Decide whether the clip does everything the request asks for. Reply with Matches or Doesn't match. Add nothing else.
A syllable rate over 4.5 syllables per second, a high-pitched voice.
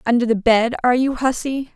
Matches